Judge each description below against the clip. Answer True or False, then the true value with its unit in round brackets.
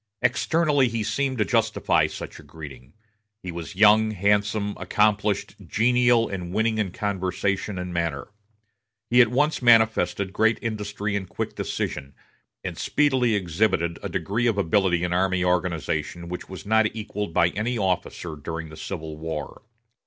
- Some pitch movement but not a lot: True (4.1 semitones)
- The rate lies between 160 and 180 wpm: False (150 wpm)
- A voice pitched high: False (100 Hz)